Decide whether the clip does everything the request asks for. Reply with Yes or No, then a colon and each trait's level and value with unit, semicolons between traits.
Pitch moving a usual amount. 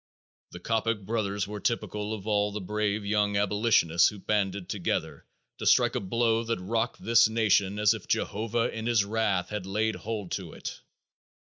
No: narrow, 1.9 semitones